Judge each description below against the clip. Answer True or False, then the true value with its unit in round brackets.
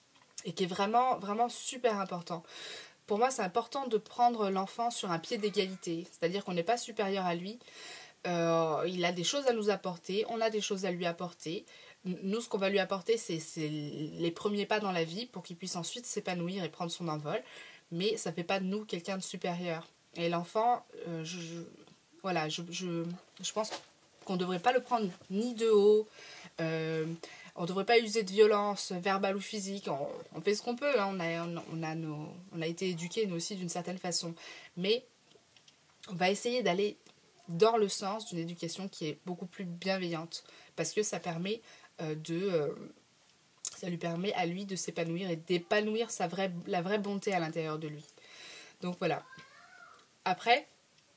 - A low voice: False (185 Hz)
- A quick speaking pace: False (195 wpm)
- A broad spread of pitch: False (3.8 semitones)